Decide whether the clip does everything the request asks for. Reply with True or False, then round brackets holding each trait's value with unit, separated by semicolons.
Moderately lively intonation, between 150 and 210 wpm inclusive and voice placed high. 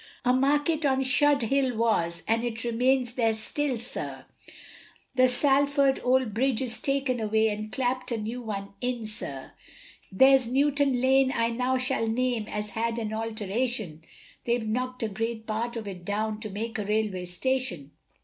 True (3.1 semitones; 160 wpm; 235 Hz)